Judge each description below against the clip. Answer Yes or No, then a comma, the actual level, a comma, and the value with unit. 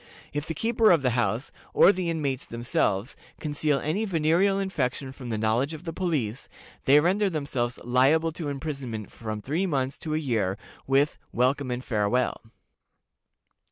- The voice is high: No, medium, 140 Hz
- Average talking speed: Yes, average, 155 wpm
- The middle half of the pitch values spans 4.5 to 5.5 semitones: Yes, average, 4.8 semitones